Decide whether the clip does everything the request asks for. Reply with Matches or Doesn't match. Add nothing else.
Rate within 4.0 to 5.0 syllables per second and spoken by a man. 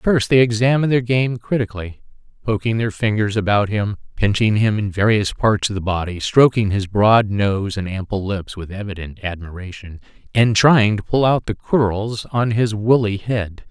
Matches